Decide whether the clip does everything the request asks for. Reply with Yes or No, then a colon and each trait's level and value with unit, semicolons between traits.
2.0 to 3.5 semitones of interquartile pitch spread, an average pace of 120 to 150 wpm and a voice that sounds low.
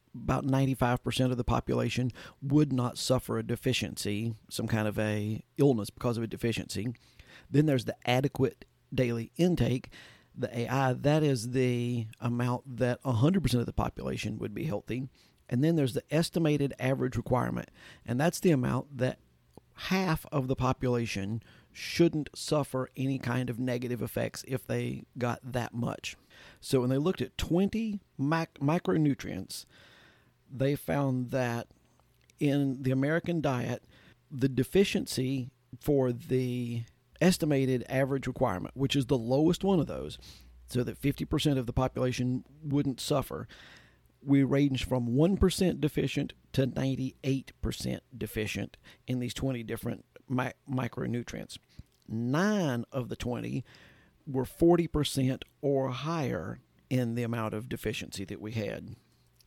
Yes: average, 2.9 semitones; slow, 135 wpm; low, 130 Hz